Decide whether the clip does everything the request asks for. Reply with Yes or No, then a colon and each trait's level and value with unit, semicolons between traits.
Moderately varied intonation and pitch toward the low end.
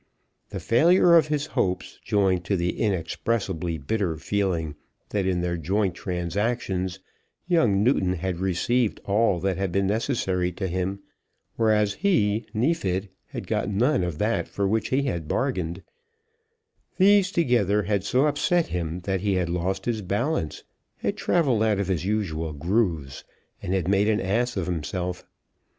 Yes: average, 4.3 semitones; low, 100 Hz